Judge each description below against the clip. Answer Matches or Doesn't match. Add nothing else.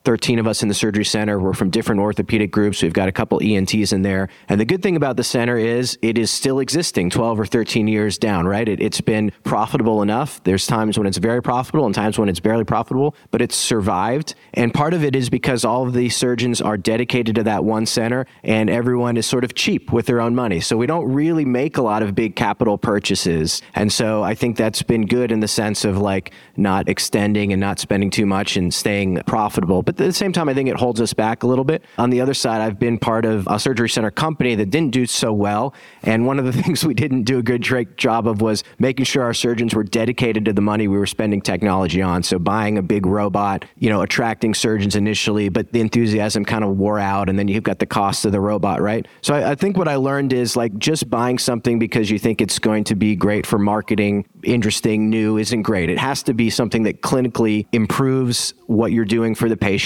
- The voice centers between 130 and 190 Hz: Doesn't match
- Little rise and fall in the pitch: Doesn't match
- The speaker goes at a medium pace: Doesn't match